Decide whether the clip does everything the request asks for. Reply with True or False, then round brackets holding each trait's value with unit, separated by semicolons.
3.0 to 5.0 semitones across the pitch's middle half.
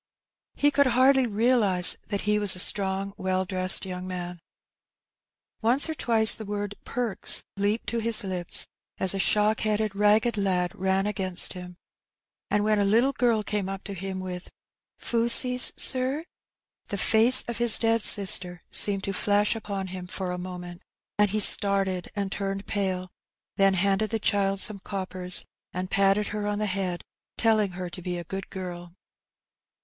False (2.6 semitones)